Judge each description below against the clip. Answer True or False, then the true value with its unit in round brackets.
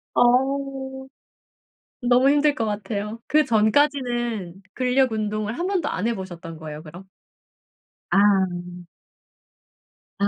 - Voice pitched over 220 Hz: True (230 Hz)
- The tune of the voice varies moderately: True (4.9 semitones)